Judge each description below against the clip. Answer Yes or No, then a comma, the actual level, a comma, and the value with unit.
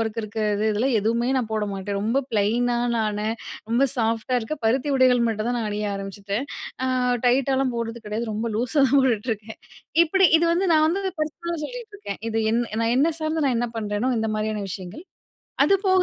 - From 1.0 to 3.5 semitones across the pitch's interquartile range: No, average, 4.2 semitones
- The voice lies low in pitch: No, high, 235 Hz